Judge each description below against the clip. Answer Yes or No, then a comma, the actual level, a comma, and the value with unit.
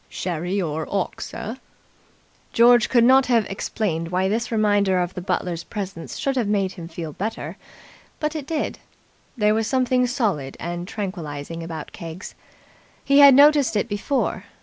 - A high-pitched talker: Yes, high, 205 Hz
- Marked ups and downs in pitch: Yes, wide, 5.7 semitones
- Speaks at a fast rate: No, average, 155 wpm